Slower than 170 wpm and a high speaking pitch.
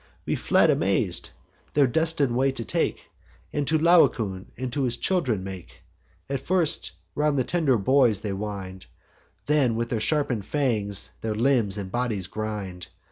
No: average, 150 wpm; low, 120 Hz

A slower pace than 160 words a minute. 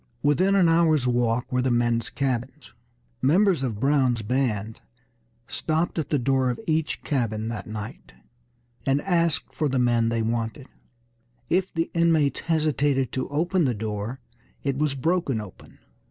Yes: average, 150 wpm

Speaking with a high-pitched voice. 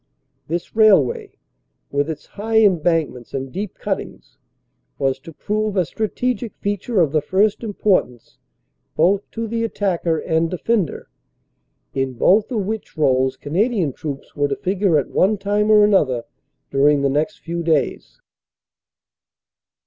No: medium, 175 Hz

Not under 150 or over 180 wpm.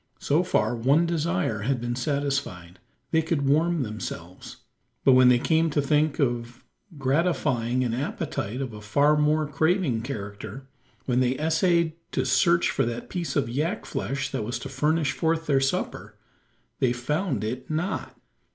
Yes: average, 160 wpm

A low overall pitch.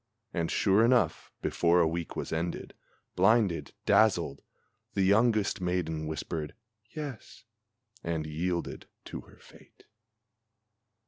Yes: very low, 90 Hz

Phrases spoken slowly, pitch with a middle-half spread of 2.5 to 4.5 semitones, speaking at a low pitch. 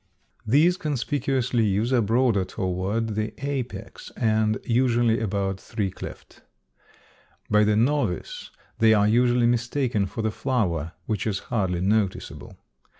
Yes: slow, 125 wpm; average, 3.3 semitones; low, 110 Hz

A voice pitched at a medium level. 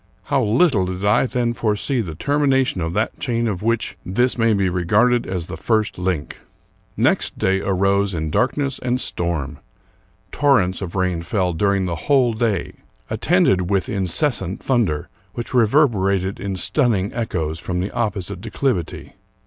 No: low, 100 Hz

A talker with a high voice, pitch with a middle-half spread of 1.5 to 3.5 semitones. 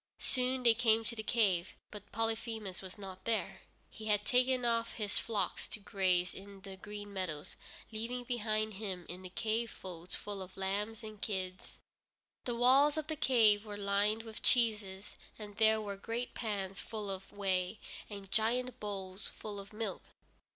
Yes: high, 210 Hz; average, 2.8 semitones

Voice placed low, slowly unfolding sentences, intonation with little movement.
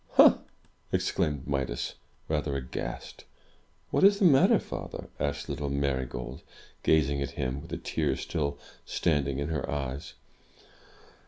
Yes: very low, 70 Hz; slow, 130 wpm; narrow, 1.8 semitones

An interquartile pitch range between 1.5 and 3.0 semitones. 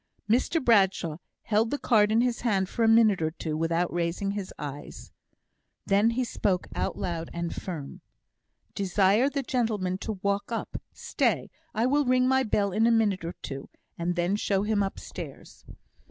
No: average, 4.5 semitones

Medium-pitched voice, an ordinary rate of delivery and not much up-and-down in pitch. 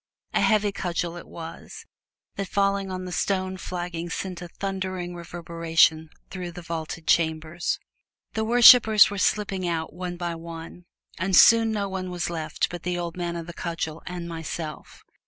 Yes: medium, 175 Hz; average, 165 wpm; narrow, 2.3 semitones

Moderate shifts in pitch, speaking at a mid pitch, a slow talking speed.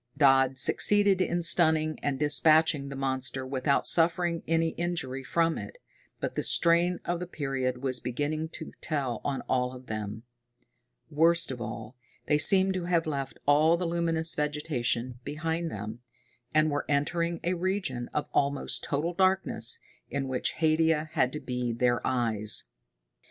No: average, 4.5 semitones; medium, 150 Hz; average, 150 wpm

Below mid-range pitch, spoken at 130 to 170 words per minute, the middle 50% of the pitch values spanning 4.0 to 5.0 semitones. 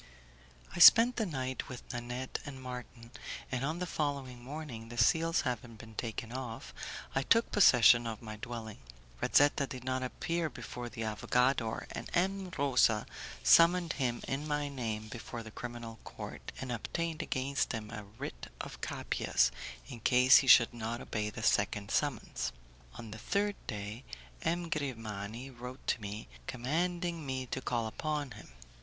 Yes: low, 125 Hz; average, 160 wpm; average, 4.3 semitones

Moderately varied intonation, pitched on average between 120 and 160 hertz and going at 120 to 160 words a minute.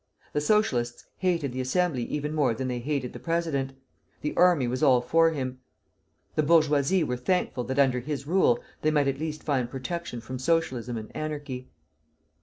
No: average, 4.0 semitones; medium, 140 Hz; average, 175 wpm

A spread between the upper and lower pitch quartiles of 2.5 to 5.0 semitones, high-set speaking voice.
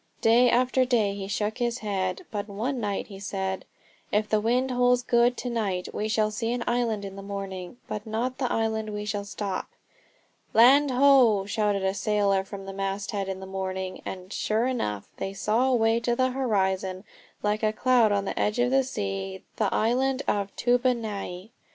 Yes: average, 3.7 semitones; high, 215 Hz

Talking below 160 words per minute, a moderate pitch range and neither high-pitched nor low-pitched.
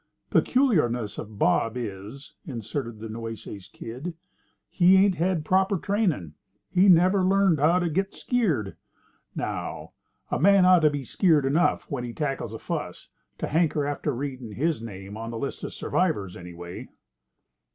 No: average, 150 wpm; wide, 8.2 semitones; medium, 145 Hz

